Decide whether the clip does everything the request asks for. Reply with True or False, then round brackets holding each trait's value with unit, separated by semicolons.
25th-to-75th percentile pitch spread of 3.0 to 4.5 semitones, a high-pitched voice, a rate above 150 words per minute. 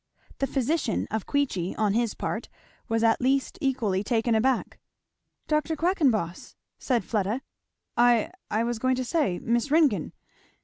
False (3.8 semitones; 240 Hz; 140 wpm)